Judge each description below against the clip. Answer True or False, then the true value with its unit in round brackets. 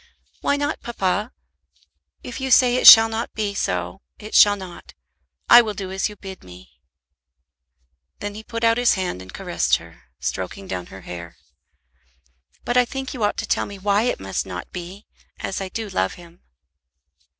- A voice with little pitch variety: False (4.9 semitones)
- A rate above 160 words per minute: True (180 wpm)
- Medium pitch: False (200 Hz)